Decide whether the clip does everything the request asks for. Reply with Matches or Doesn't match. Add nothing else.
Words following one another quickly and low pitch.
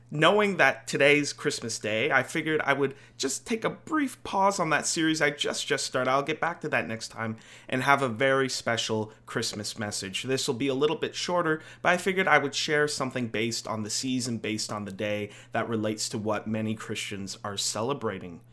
Matches